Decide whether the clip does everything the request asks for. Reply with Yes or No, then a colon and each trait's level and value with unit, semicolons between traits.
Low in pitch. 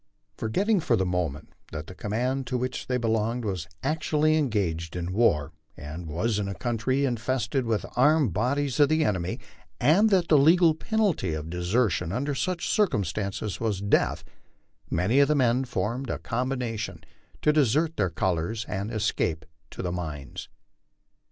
Yes: low, 115 Hz